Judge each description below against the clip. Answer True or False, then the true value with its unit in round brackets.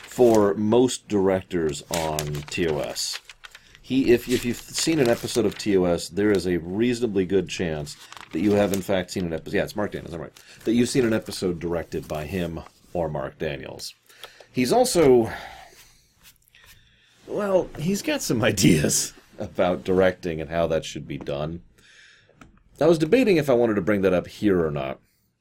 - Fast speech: False (170 wpm)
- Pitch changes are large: True (5.9 semitones)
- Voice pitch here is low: True (100 Hz)